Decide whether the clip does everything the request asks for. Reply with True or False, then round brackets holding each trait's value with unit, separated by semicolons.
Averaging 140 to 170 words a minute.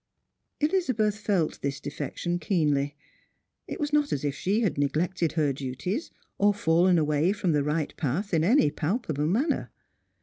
True (155 wpm)